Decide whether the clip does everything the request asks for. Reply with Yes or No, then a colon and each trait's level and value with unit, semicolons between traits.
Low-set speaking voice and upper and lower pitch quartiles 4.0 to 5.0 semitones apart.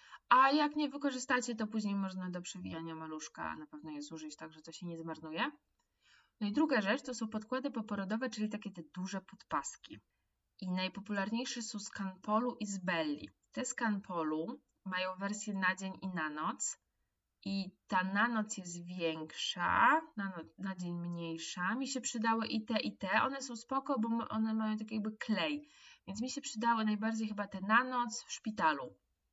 No: high, 210 Hz; average, 4.3 semitones